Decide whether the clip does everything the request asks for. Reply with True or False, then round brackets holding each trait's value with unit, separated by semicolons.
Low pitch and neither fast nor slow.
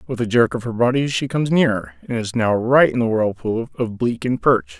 False (115 Hz; 250 wpm)